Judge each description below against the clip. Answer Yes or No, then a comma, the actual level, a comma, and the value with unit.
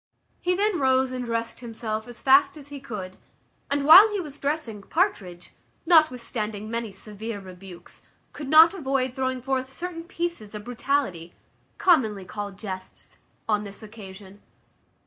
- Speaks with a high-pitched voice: Yes, high, 245 Hz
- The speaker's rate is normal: Yes, average, 145 wpm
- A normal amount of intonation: No, wide, 5.7 semitones